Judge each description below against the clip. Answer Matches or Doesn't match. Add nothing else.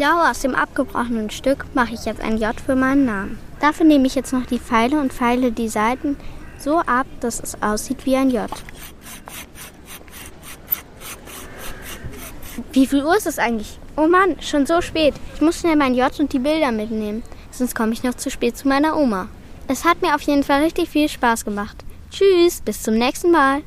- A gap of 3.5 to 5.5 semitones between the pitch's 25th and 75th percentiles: Matches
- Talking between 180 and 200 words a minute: Matches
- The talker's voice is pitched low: Doesn't match